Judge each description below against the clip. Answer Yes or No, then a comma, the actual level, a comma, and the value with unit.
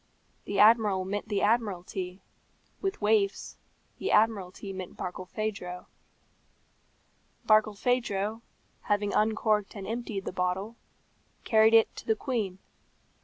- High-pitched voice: Yes, high, 205 Hz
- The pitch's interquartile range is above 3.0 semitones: No, narrow, 2.4 semitones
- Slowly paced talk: Yes, slow, 105 wpm